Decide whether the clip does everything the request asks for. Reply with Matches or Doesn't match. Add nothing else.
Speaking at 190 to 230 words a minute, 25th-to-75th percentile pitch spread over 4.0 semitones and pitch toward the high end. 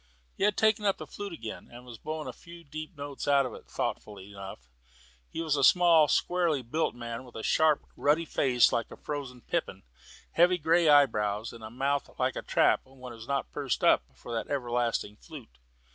Doesn't match